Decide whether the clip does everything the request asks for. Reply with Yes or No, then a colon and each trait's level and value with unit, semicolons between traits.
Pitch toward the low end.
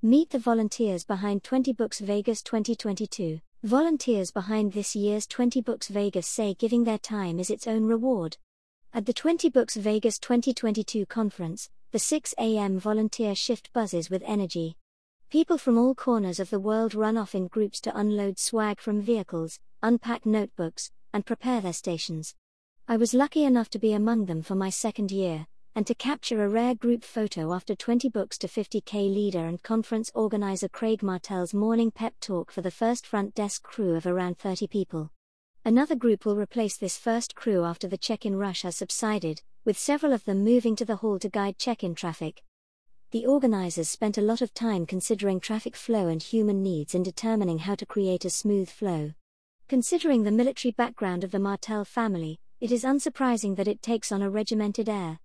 No: high, 215 Hz